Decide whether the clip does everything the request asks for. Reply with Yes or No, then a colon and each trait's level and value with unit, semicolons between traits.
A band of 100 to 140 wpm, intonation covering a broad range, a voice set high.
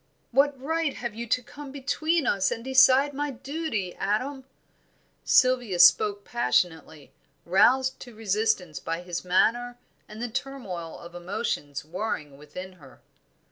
Yes: slow, 135 wpm; wide, 6.8 semitones; high, 225 Hz